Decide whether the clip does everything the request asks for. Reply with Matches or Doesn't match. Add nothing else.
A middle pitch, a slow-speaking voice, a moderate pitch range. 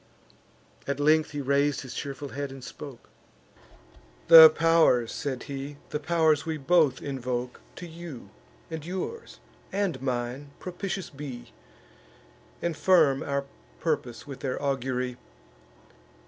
Matches